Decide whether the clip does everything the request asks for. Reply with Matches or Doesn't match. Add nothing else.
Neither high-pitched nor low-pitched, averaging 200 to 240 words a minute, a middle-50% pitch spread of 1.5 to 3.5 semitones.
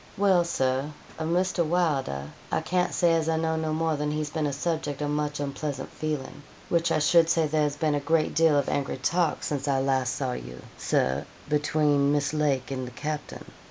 Matches